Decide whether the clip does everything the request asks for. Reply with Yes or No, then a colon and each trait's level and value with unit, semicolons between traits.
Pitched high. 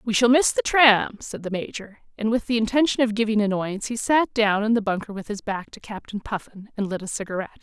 Yes: high, 220 Hz